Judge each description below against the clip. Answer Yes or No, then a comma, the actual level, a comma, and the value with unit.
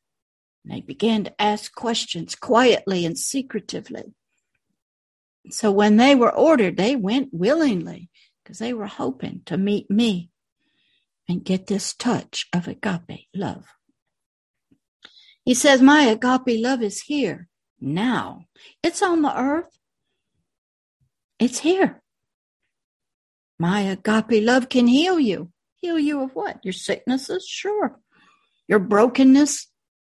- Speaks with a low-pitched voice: No, high, 230 Hz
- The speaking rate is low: Yes, slow, 115 wpm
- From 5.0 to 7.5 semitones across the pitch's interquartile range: Yes, wide, 5.4 semitones